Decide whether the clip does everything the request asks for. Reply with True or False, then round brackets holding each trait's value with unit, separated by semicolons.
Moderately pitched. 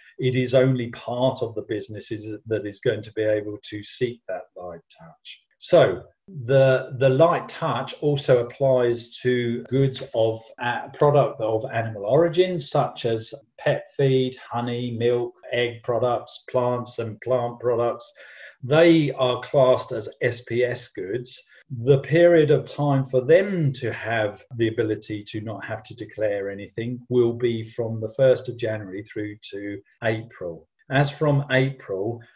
False (125 Hz)